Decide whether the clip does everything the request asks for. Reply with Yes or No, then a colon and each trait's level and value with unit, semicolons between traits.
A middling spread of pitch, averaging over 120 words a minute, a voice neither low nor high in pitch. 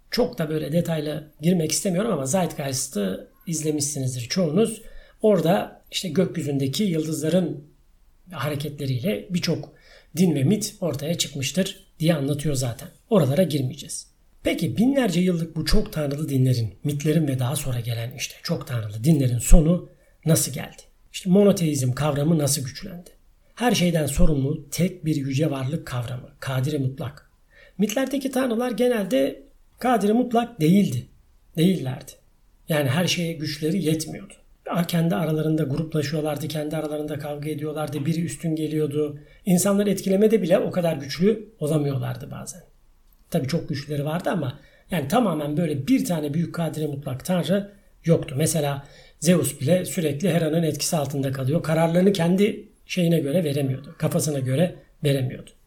Yes: average, 3.7 semitones; average, 130 wpm; medium, 160 Hz